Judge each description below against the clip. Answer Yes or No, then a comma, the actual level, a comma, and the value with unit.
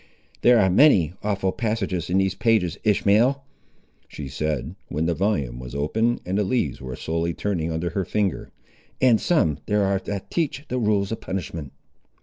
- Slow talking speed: No, average, 170 wpm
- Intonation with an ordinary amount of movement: Yes, average, 4.9 semitones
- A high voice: No, very low, 95 Hz